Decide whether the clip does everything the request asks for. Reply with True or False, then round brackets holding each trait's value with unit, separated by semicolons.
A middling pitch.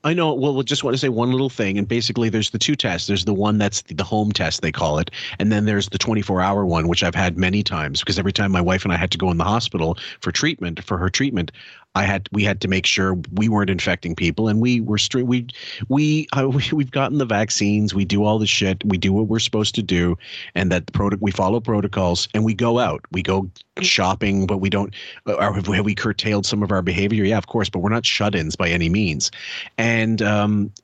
False (105 Hz)